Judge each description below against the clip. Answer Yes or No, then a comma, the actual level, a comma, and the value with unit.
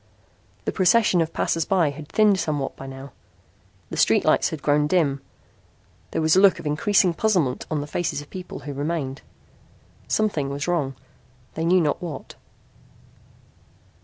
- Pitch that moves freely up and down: No, average, 3.9 semitones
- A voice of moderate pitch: Yes, medium, 160 Hz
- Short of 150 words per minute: No, average, 160 wpm